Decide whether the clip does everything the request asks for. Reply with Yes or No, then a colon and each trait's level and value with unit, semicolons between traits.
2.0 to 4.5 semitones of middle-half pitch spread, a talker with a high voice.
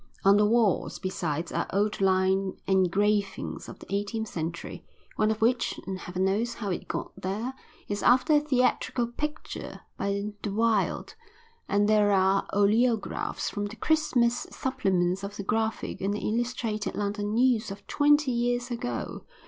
Yes: average, 3.5 semitones; high, 210 Hz